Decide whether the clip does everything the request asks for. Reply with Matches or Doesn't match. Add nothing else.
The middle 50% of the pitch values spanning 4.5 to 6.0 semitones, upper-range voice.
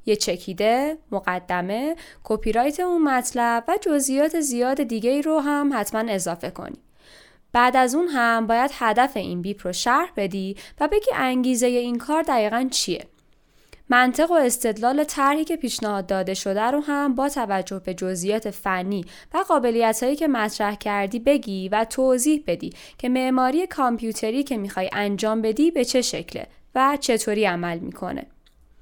Matches